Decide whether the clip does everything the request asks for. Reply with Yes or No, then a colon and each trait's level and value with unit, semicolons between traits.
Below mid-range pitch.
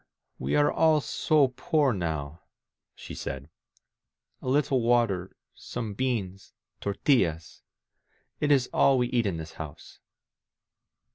Yes: low, 120 Hz